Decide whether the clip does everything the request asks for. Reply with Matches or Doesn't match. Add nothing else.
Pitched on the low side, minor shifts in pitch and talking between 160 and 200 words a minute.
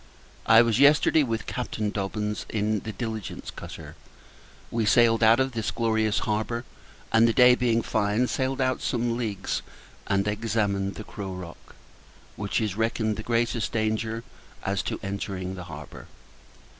Doesn't match